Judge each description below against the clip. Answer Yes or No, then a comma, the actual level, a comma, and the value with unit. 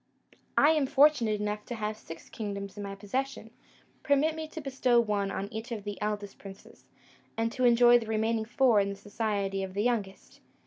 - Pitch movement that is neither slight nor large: Yes, average, 3.3 semitones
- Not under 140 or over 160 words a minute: No, average, 190 wpm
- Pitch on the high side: Yes, high, 220 Hz